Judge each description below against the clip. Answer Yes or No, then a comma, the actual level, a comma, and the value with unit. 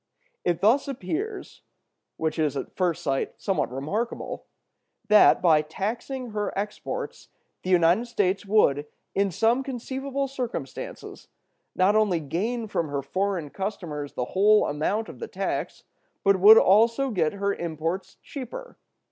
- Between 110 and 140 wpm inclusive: Yes, slow, 135 wpm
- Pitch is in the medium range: No, high, 200 Hz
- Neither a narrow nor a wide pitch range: No, wide, 5.9 semitones